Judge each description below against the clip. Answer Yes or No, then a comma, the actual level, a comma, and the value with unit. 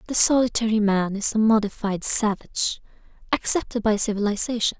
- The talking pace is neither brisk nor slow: No, slow, 125 wpm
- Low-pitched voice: No, high, 215 Hz